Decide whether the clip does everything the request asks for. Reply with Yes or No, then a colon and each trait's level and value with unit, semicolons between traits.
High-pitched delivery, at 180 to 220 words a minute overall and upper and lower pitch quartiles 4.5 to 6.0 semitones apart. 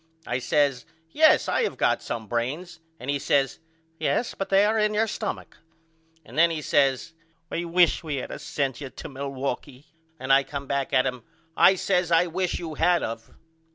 No: medium, 145 Hz; average, 195 wpm; average, 5.0 semitones